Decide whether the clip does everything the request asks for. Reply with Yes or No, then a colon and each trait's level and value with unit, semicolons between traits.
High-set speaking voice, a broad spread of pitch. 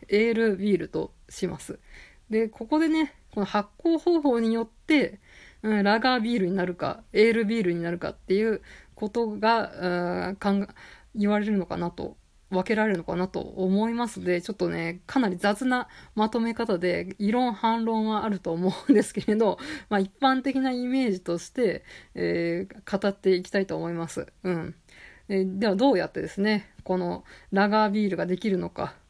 No: high, 210 Hz; average, 3.5 semitones